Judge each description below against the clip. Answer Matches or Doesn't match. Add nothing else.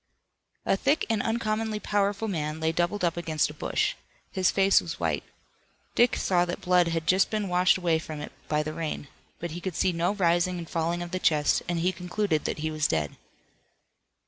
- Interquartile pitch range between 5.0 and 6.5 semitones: Doesn't match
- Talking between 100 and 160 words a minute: Doesn't match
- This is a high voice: Doesn't match